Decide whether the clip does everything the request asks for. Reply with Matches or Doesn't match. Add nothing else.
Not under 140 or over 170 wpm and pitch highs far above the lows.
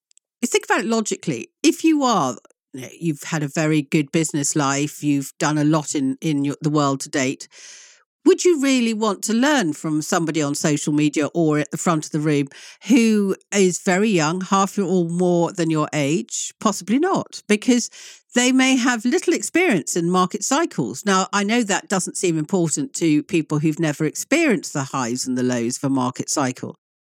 Doesn't match